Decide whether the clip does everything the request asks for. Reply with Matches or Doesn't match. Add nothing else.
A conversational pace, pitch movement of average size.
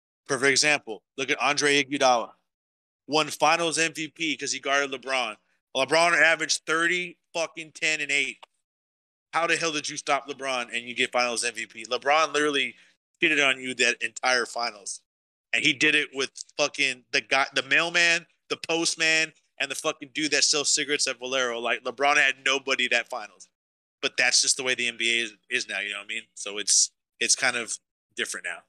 Matches